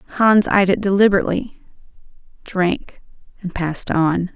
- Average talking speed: No, slow, 110 wpm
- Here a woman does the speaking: Yes, female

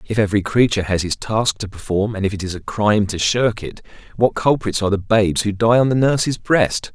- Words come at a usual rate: No, fast, 240 wpm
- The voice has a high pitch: No, low, 105 Hz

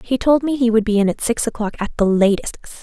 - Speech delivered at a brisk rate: Yes, fast, 275 wpm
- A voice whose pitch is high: Yes, high, 225 Hz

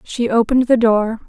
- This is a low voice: No, high, 230 Hz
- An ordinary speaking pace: Yes, average, 190 wpm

